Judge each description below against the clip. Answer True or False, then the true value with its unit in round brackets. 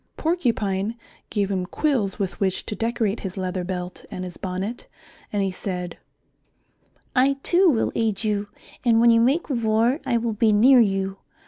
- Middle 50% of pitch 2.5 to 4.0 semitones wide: True (3.6 semitones)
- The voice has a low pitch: False (210 Hz)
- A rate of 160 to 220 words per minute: True (165 wpm)